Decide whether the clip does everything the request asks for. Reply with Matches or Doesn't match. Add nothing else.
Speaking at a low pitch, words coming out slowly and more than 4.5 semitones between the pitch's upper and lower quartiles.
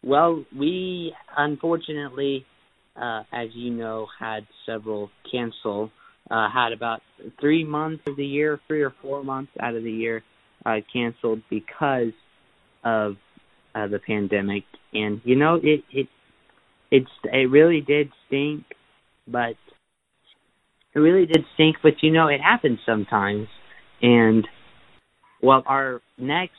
Matches